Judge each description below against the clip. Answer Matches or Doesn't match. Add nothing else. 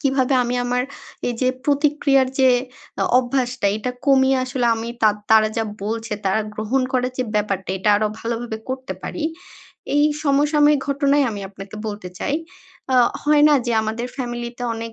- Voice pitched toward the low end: Doesn't match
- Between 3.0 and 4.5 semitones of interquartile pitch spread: Matches